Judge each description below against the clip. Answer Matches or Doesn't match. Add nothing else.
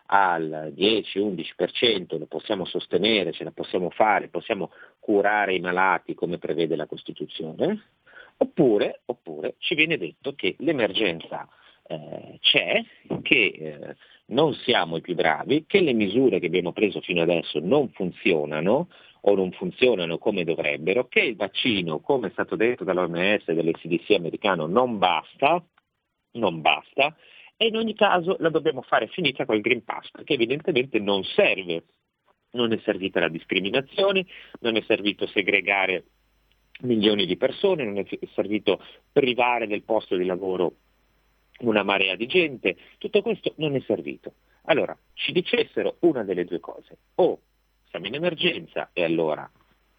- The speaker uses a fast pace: Doesn't match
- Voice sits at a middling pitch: Doesn't match